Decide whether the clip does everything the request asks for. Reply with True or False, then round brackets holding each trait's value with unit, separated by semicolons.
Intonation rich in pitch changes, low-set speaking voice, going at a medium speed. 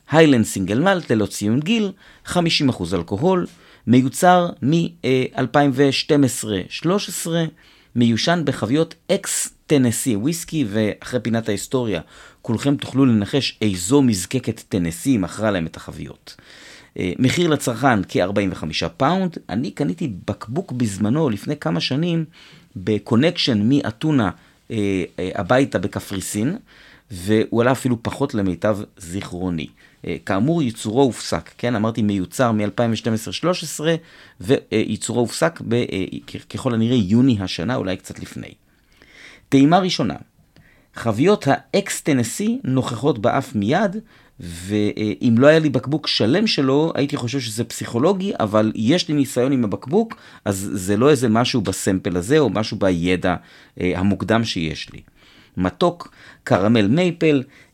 True (6.2 semitones; 120 Hz; 115 wpm)